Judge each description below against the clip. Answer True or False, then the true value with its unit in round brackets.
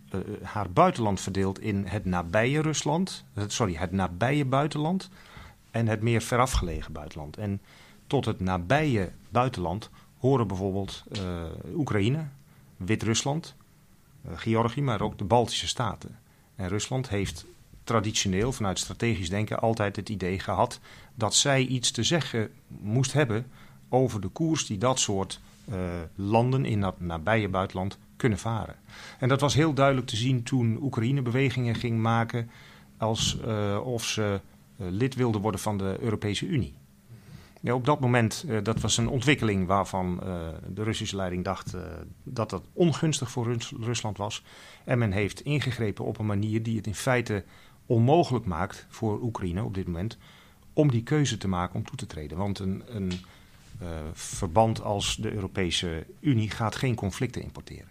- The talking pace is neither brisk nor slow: True (160 wpm)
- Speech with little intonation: False (4.7 semitones)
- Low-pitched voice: True (110 Hz)